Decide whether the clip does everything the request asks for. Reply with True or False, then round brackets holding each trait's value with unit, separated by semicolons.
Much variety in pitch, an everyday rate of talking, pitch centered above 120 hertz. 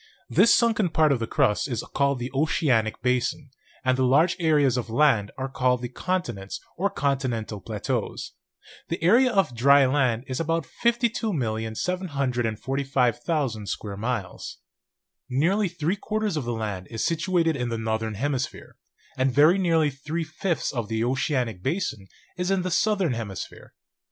True (6.0 semitones; 155 wpm; 135 Hz)